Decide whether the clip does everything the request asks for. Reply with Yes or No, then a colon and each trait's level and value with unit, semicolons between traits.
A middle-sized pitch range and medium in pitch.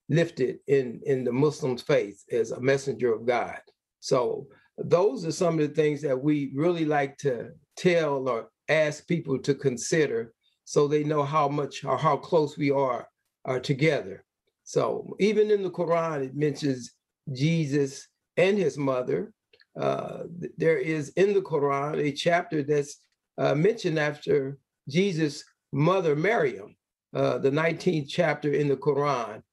Yes: average, 3.6 semitones; medium, 150 Hz